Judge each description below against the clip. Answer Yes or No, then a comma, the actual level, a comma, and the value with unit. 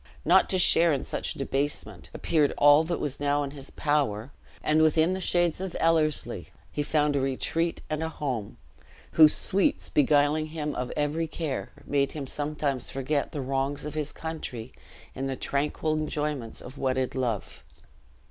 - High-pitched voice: No, medium, 145 Hz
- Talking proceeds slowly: No, average, 165 wpm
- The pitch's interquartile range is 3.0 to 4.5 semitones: No, narrow, 2.4 semitones